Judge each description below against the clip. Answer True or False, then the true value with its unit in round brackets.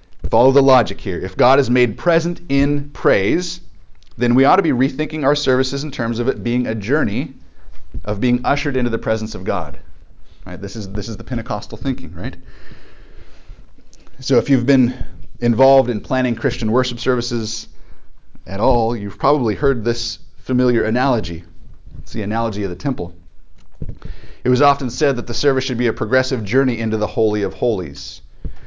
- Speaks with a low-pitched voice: True (120 Hz)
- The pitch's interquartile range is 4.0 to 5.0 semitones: True (4.4 semitones)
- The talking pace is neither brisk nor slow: True (175 wpm)